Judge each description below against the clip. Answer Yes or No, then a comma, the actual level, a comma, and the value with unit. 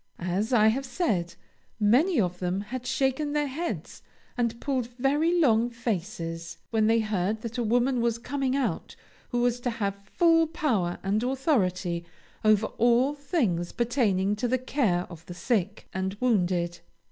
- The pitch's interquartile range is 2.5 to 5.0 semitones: No, wide, 5.4 semitones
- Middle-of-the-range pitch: No, high, 230 Hz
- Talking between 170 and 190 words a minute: No, average, 160 wpm